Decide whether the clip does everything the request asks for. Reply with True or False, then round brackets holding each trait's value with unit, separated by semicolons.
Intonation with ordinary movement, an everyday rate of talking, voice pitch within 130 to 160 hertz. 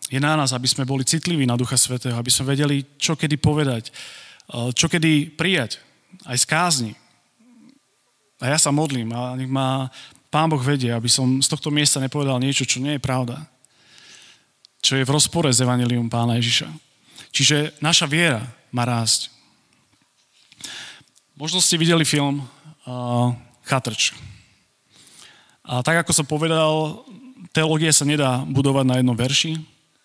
True (3.8 semitones; 150 wpm; 140 Hz)